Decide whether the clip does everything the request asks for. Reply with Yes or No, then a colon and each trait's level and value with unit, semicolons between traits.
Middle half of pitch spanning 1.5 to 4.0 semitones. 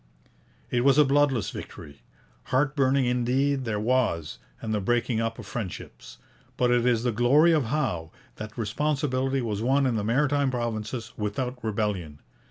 Yes: average, 3.6 semitones